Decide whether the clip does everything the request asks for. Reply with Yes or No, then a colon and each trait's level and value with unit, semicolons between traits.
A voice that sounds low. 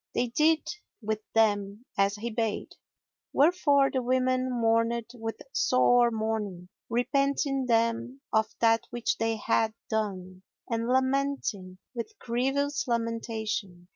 No: high, 230 Hz